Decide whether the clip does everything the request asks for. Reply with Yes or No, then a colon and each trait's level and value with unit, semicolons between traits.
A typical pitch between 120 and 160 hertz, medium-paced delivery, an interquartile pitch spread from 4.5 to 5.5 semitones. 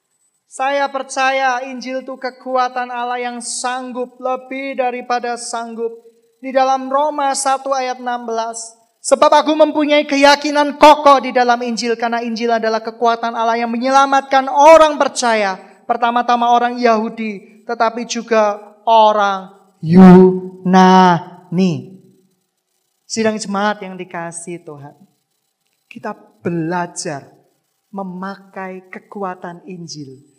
No: high, 230 Hz; average, 100 wpm; average, 4.9 semitones